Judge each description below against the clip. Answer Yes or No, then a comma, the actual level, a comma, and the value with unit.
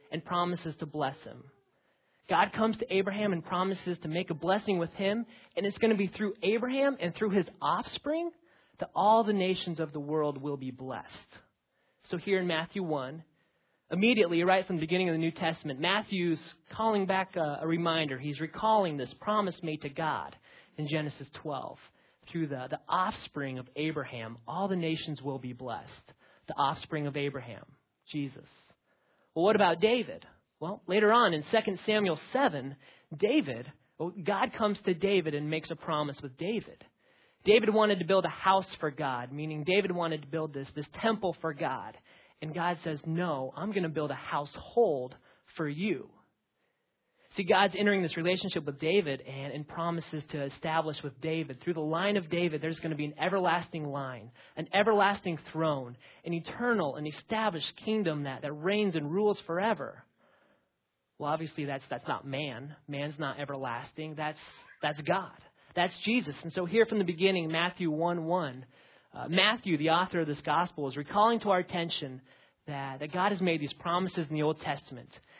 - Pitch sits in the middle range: Yes, medium, 165 Hz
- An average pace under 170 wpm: No, average, 175 wpm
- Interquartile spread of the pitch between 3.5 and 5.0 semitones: Yes, average, 4.6 semitones